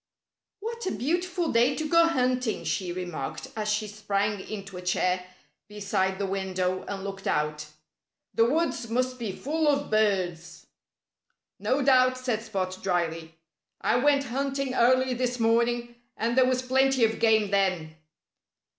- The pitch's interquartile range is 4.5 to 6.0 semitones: Yes, average, 5.1 semitones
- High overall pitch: Yes, high, 225 Hz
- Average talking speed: Yes, average, 145 wpm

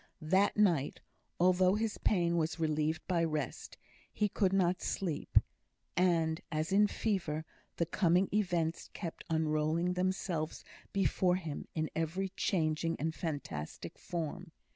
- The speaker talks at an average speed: No, slow, 125 wpm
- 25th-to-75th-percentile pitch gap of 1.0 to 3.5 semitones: Yes, average, 2.9 semitones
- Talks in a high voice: No, medium, 170 Hz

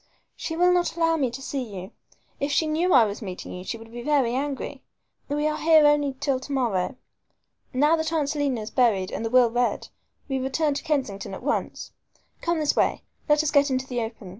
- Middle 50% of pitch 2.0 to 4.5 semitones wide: Yes, average, 4.2 semitones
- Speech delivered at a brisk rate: Yes, fast, 215 wpm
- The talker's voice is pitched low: No, very high, 270 Hz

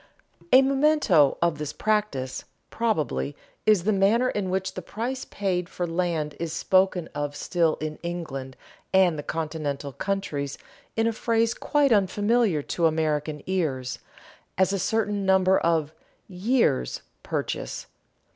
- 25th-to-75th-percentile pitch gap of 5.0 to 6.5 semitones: Yes, wide, 5.5 semitones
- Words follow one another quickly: No, slow, 135 wpm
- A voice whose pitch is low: No, medium, 180 Hz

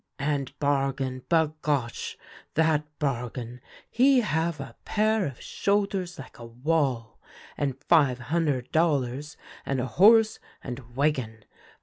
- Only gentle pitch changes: No, average, 4.6 semitones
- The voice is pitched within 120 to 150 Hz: Yes, medium, 140 Hz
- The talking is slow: Yes, slow, 115 wpm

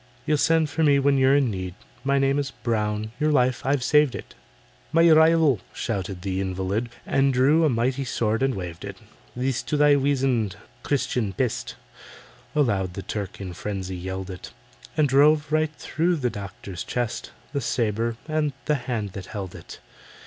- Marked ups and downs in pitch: Yes, wide, 6.2 semitones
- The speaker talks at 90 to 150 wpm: No, average, 170 wpm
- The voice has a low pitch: Yes, low, 125 Hz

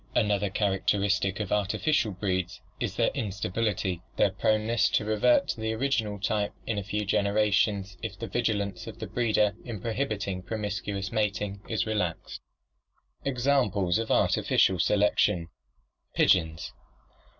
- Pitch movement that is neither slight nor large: No, narrow, 2.2 semitones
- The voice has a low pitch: Yes, low, 105 Hz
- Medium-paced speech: No, slow, 130 wpm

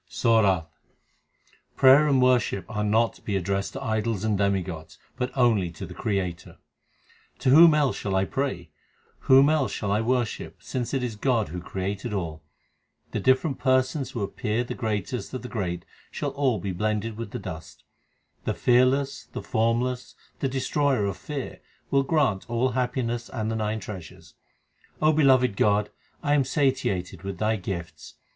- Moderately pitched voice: No, low, 115 Hz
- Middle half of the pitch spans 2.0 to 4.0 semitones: No, average, 4.9 semitones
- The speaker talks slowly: No, average, 165 wpm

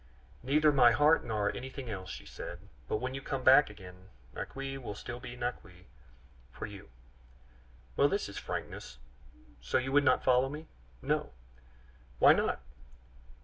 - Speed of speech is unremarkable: Yes, average, 150 wpm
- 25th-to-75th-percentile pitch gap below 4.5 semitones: No, average, 4.8 semitones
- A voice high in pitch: No, low, 125 Hz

